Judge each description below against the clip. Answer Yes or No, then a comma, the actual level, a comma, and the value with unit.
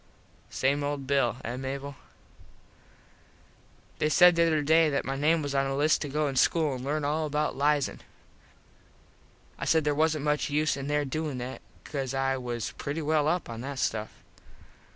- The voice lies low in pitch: No, medium, 145 Hz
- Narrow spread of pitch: Yes, narrow, 2.2 semitones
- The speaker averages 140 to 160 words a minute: No, average, 180 wpm